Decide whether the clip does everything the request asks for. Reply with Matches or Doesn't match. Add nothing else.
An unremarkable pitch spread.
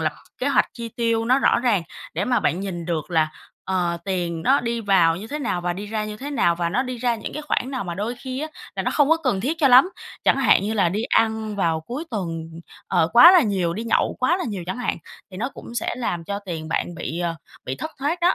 Doesn't match